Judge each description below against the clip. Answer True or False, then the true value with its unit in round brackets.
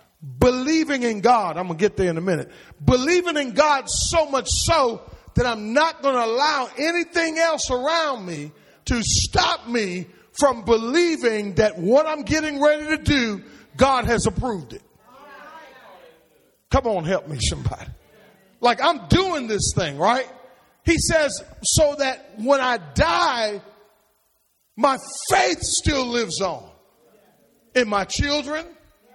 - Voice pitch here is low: False (250 Hz)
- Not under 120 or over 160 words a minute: True (140 wpm)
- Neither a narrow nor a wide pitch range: False (6.1 semitones)